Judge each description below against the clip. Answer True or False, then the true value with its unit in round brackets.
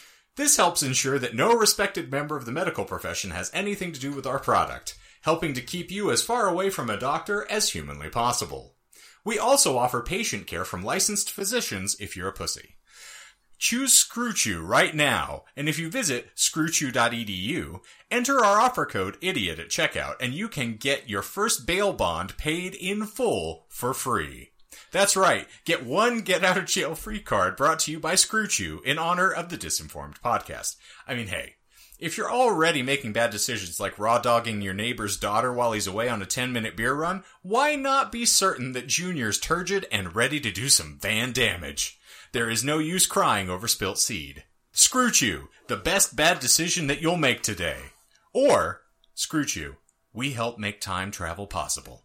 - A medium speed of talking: True (180 wpm)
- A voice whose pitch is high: False (140 Hz)